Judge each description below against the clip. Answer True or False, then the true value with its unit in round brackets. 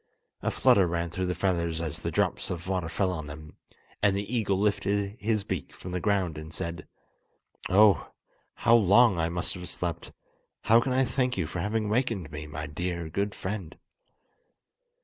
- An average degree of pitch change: True (3.6 semitones)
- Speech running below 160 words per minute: False (180 wpm)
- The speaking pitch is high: False (95 Hz)